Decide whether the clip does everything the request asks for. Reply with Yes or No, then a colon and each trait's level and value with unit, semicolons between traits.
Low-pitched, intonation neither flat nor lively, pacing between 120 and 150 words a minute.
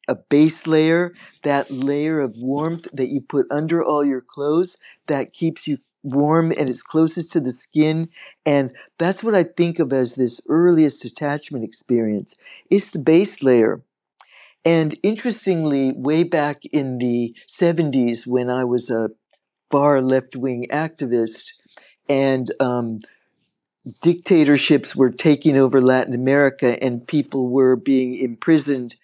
No: medium, 145 Hz; average, 4.0 semitones; average, 140 wpm